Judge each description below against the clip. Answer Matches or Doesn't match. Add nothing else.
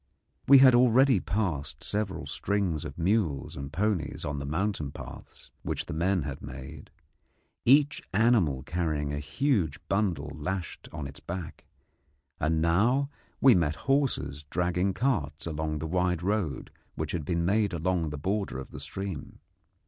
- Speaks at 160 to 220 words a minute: Doesn't match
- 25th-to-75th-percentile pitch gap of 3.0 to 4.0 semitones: Doesn't match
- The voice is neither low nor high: Doesn't match